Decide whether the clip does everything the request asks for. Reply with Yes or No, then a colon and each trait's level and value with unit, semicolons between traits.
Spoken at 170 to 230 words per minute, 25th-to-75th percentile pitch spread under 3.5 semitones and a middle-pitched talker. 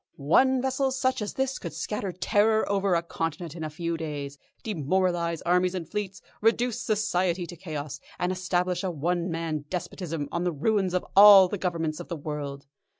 No: average, 180 wpm; average, 3.8 semitones; medium, 180 Hz